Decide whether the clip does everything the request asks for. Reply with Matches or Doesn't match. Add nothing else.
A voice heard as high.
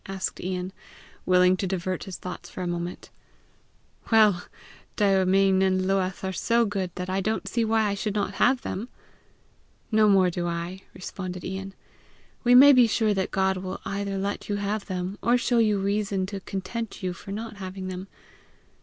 Matches